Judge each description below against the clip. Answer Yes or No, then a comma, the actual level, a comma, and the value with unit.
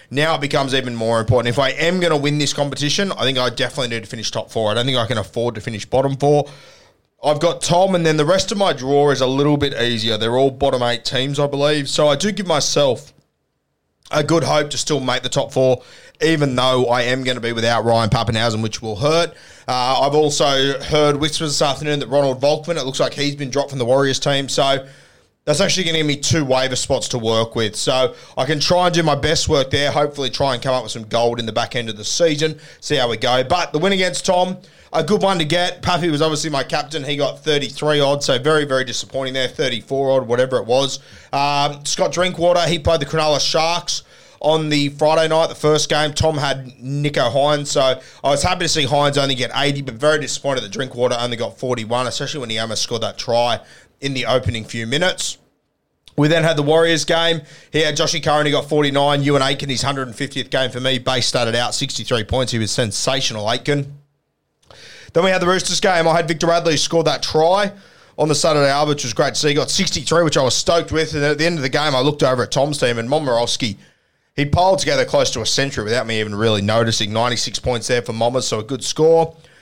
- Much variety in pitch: No, average, 3.7 semitones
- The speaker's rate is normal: No, fast, 240 wpm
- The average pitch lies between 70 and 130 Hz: No, medium, 140 Hz